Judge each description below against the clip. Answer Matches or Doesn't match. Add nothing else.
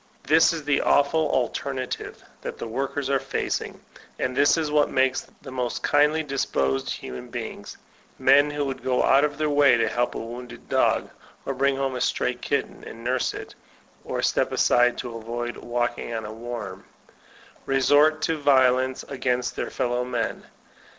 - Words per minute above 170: Matches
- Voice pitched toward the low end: Matches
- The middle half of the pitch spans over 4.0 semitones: Doesn't match